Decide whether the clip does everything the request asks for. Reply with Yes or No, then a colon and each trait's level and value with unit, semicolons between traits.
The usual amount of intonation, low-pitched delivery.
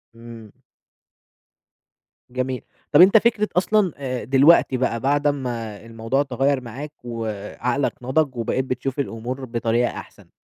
Yes: average, 3.4 semitones; low, 130 Hz